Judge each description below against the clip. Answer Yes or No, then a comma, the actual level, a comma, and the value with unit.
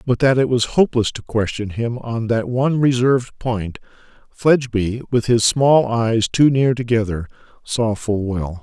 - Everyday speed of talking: Yes, average, 165 wpm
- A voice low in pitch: Yes, low, 120 Hz